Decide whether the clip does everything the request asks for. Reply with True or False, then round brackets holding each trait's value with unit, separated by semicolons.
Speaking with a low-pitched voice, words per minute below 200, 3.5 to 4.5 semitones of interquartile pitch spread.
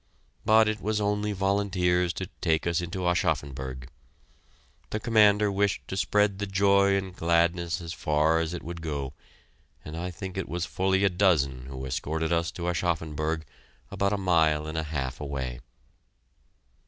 True (85 Hz; 160 wpm; 3.9 semitones)